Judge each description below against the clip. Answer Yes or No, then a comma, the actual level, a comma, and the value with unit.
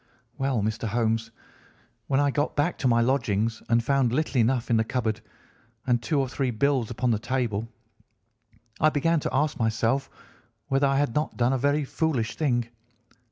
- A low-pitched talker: Yes, low, 125 Hz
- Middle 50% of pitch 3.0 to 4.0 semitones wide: Yes, average, 3.4 semitones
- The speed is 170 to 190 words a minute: Yes, average, 175 wpm